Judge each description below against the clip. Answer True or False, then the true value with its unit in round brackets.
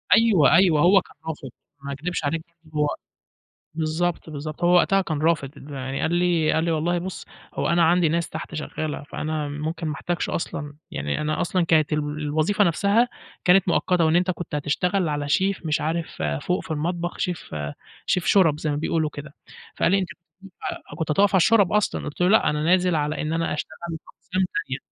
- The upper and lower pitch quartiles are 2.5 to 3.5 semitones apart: True (2.9 semitones)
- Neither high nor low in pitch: True (160 Hz)